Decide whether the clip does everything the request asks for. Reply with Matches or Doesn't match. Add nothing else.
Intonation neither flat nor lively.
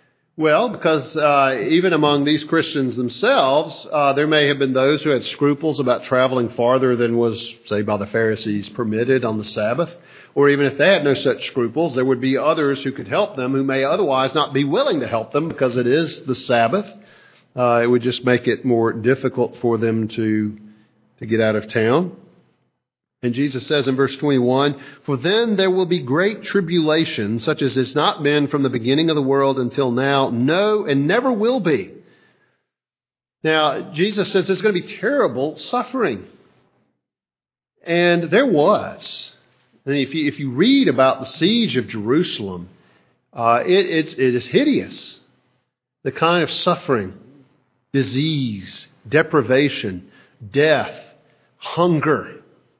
Matches